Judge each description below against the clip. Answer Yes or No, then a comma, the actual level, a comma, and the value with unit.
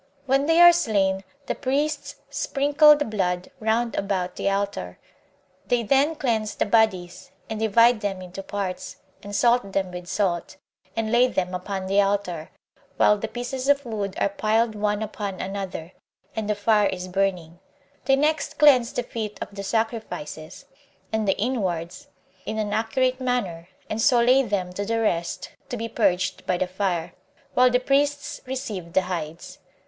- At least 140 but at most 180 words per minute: Yes, average, 165 wpm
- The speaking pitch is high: Yes, high, 210 Hz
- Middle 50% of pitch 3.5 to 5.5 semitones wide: Yes, average, 4.6 semitones